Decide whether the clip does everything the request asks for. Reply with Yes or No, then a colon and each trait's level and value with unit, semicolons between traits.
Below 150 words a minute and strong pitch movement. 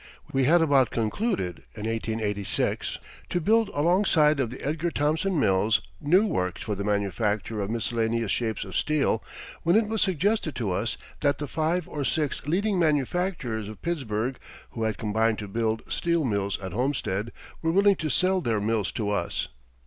No: average, 170 wpm; wide, 7.5 semitones